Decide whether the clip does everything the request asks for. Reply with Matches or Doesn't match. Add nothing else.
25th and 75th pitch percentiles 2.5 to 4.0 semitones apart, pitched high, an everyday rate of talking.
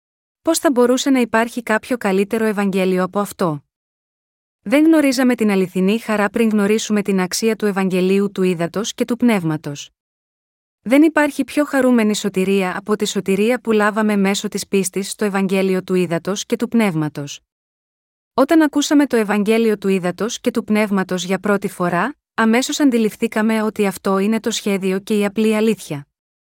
Matches